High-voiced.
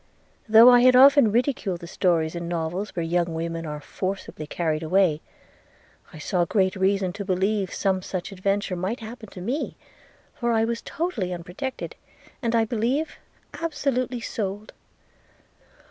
Yes: high, 195 Hz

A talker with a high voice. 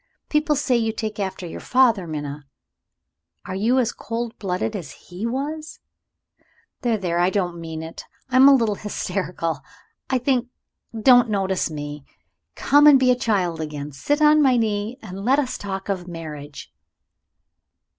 Yes: high, 205 Hz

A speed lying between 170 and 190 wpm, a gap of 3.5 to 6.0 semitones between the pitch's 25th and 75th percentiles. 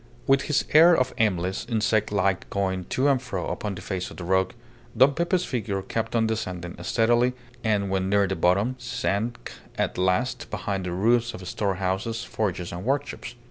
Yes: average, 180 wpm; average, 4.3 semitones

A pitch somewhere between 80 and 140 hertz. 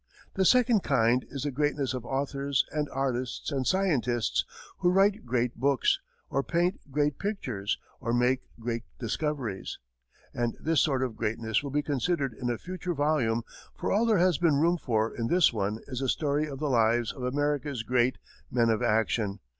Yes: low, 135 Hz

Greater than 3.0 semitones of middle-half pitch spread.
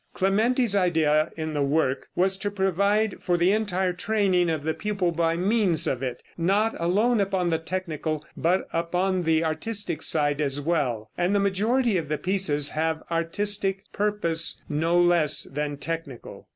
Yes: average, 3.9 semitones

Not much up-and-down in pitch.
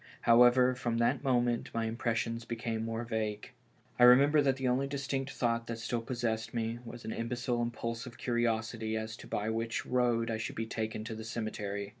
Yes: narrow, 1.5 semitones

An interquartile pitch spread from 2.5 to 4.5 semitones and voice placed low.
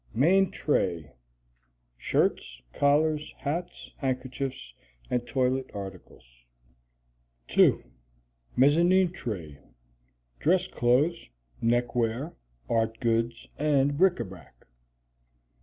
No: average, 5.1 semitones; low, 130 Hz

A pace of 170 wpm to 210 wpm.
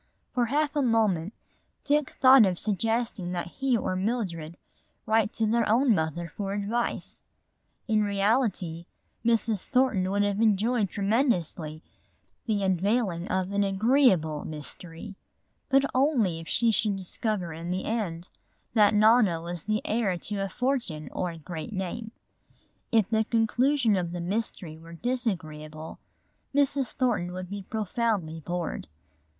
No: average, 140 wpm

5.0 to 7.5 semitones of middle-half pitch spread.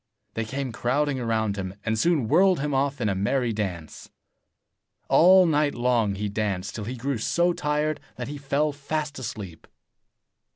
Yes: wide, 5.5 semitones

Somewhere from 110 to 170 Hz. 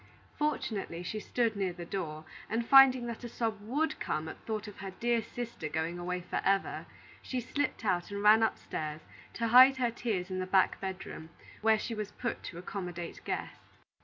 No: high, 210 Hz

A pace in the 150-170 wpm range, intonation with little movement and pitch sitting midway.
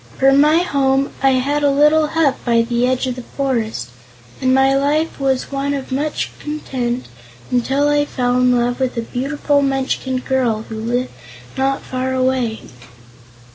No: average, 165 wpm; narrow, 2.1 semitones; very high, 265 Hz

